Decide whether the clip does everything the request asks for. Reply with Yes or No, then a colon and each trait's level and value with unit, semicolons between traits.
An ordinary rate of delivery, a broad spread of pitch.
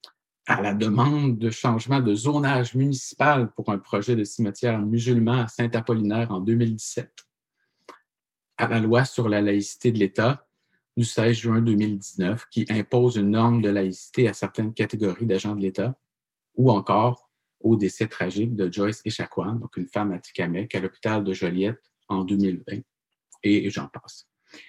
No: average, 155 wpm; average, 2.8 semitones